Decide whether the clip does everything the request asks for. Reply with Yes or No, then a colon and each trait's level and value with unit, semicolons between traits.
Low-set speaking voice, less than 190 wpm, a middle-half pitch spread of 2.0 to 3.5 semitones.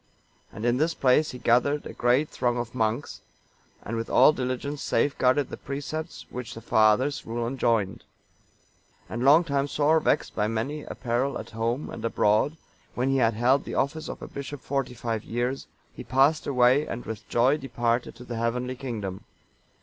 Yes: low, 125 Hz; average, 180 wpm; average, 3.2 semitones